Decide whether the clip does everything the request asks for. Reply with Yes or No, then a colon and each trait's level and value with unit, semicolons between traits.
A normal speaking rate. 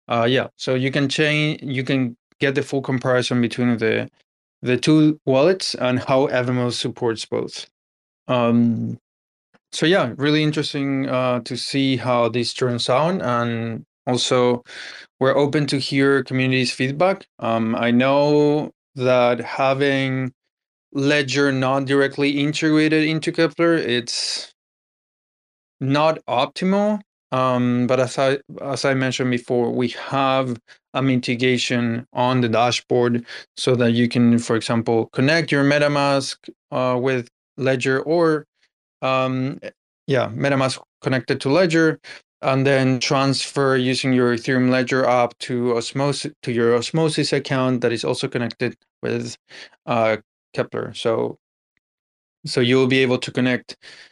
No: slow, 130 wpm